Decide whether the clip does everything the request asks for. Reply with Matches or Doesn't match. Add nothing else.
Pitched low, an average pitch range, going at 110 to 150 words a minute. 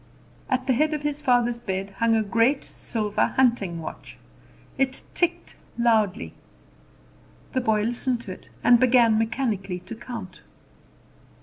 Doesn't match